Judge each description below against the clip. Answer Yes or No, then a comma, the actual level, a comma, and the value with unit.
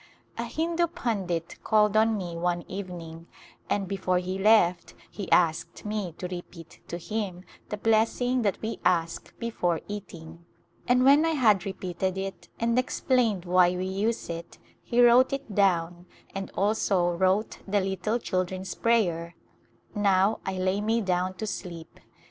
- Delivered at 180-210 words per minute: No, average, 160 wpm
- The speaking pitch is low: No, high, 190 Hz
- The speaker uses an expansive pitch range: No, average, 3.8 semitones